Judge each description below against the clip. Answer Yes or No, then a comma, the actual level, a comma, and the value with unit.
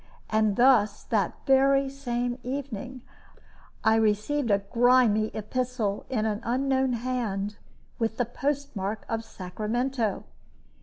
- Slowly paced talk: Yes, slow, 110 wpm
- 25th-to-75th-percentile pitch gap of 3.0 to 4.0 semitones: Yes, average, 3.4 semitones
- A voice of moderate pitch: No, high, 240 Hz